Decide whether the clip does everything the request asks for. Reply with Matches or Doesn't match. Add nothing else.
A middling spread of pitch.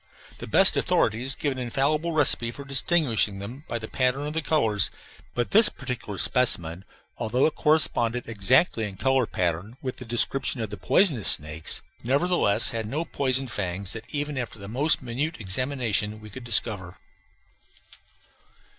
Matches